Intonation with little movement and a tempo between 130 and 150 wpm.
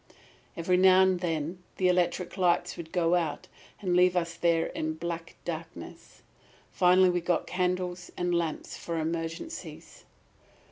Yes: narrow, 1.4 semitones; average, 140 wpm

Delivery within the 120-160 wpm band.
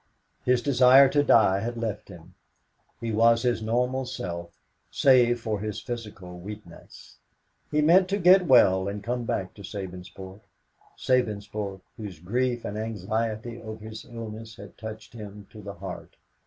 Yes: average, 150 wpm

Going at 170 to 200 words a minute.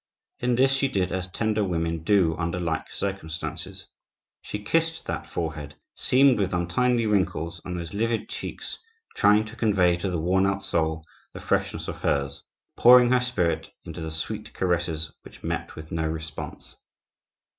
No: average, 155 wpm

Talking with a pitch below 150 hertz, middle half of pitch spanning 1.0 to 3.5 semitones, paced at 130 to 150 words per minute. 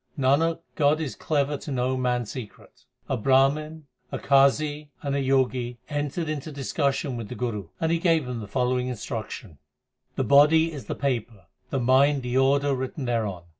No: low, 135 Hz; average, 2.9 semitones; average, 180 wpm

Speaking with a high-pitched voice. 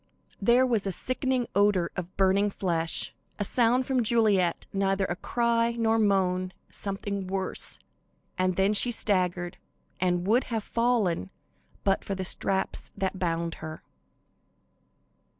Yes: high, 195 Hz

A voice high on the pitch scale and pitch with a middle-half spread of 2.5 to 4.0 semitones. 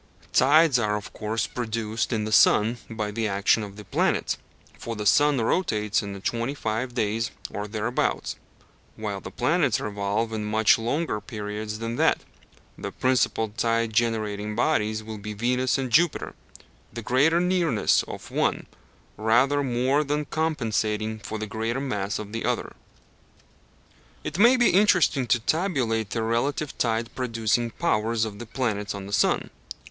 No: low, 115 Hz; average, 3.5 semitones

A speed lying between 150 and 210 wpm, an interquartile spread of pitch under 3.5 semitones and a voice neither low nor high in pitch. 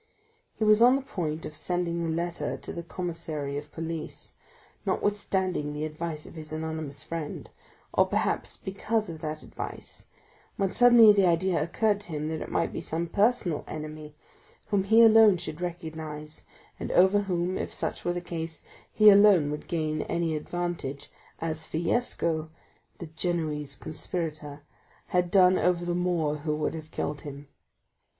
Yes: average, 155 wpm; average, 3.1 semitones; medium, 165 Hz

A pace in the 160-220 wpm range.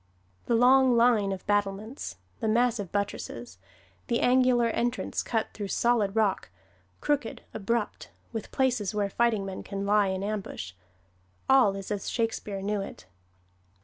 No: average, 140 wpm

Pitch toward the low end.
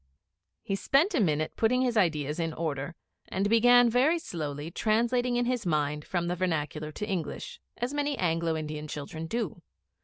No: medium, 180 Hz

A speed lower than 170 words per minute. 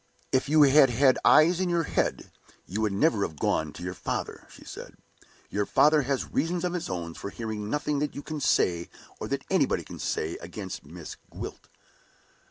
No: average, 190 wpm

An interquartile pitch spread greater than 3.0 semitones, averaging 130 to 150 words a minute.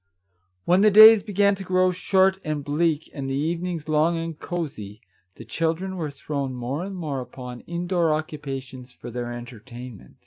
No: average, 5.3 semitones; average, 165 wpm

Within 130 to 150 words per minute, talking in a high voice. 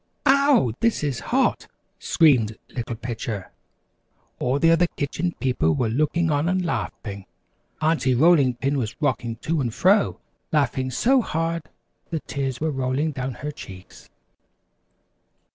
No: slow, 135 wpm; medium, 140 Hz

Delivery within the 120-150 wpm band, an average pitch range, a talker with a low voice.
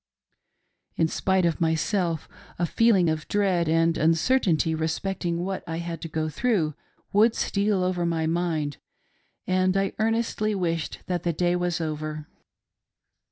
No: average, 140 wpm; average, 3.0 semitones; medium, 170 Hz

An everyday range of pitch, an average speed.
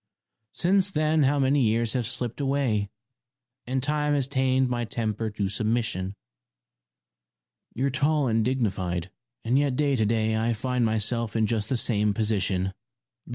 Yes: average, 3.9 semitones; average, 145 wpm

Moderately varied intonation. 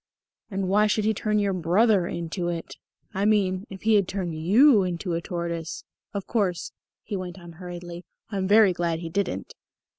Yes: average, 3.0 semitones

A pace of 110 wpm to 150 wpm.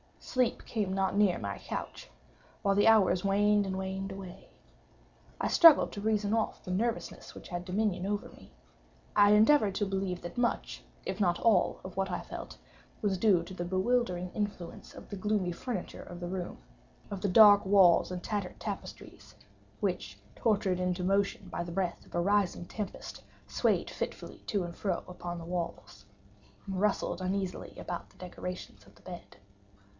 No: average, 165 wpm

